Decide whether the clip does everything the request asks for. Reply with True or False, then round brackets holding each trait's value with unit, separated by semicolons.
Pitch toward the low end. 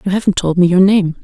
False (185 Hz)